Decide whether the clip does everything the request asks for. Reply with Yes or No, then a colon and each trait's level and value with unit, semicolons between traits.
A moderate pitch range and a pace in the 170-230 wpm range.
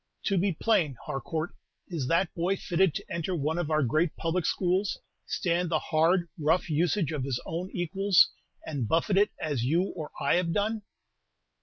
Yes: average, 3.1 semitones; average, 175 wpm